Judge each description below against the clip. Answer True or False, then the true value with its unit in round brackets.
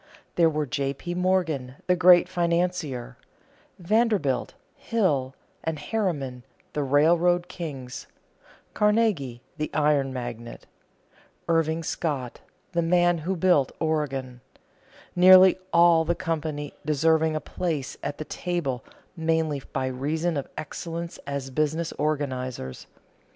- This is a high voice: False (155 Hz)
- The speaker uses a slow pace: True (115 wpm)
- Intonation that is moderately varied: True (4.2 semitones)